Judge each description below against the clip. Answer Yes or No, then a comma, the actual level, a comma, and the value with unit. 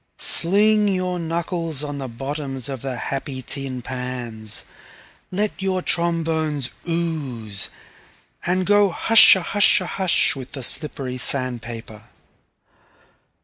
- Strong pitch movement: Yes, wide, 5.8 semitones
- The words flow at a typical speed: No, slow, 105 wpm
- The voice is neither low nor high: Yes, medium, 145 Hz